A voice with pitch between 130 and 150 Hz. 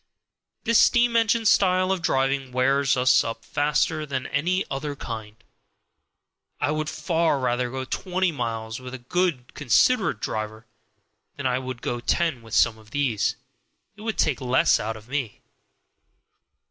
Yes: low, 135 Hz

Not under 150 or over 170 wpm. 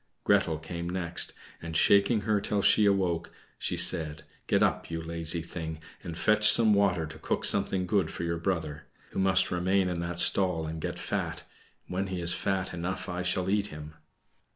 No: average, 185 wpm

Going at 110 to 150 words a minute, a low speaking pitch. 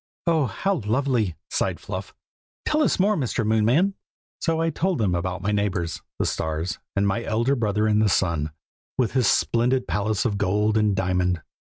No: average, 175 wpm; low, 110 Hz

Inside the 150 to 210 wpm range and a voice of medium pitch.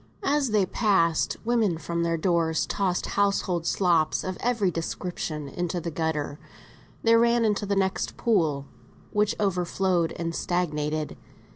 No: slow, 135 wpm; medium, 180 Hz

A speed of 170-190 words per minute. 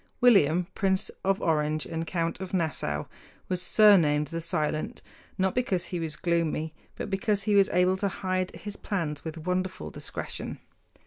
No: average, 155 wpm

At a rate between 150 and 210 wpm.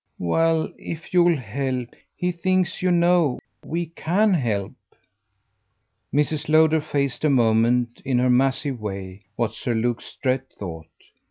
No: slow, 135 wpm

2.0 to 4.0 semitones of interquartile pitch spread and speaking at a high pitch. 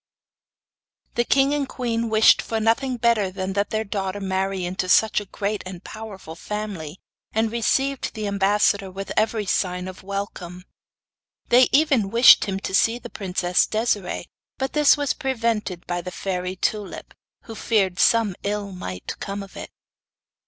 Yes: average, 3.4 semitones; high, 205 Hz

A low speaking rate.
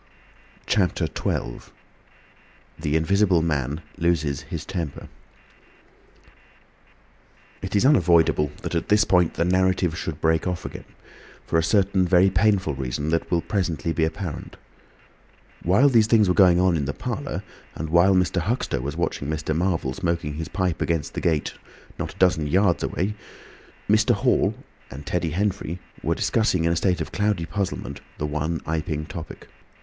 No: average, 155 wpm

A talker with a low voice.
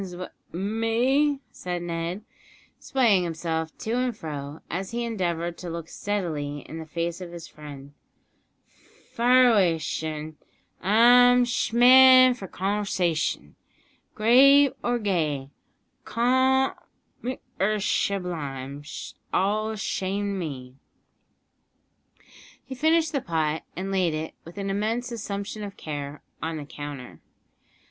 No: high, 190 Hz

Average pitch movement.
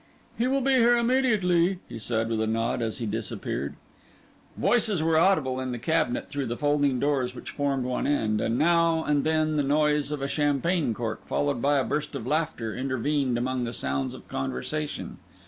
Yes: average, 4.9 semitones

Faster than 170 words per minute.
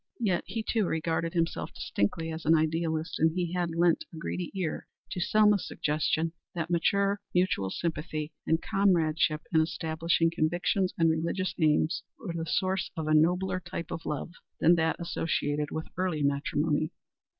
No: average, 160 wpm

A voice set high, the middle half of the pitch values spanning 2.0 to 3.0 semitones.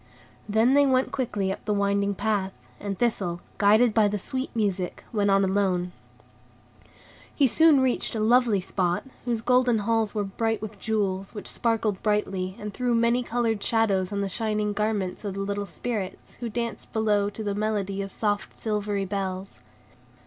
Yes: high, 210 Hz; narrow, 2.4 semitones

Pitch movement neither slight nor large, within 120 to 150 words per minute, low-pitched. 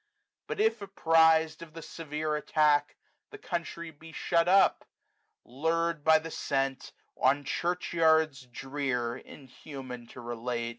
No: average, 3.5 semitones; average, 140 wpm; medium, 155 Hz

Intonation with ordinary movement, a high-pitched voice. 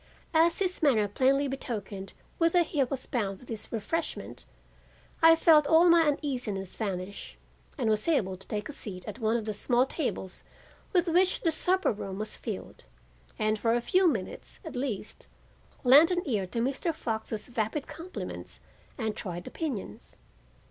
No: wide, 7.3 semitones; high, 245 Hz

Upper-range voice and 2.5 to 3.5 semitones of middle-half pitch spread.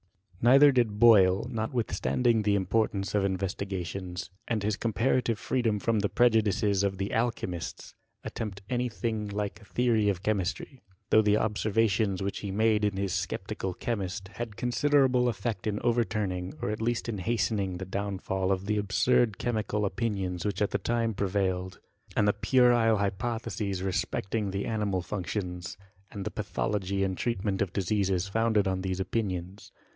No: low, 105 Hz; average, 2.9 semitones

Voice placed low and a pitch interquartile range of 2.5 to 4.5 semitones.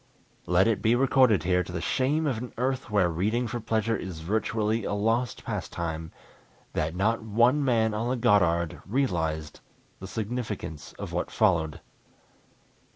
No: low, 110 Hz; wide, 5.4 semitones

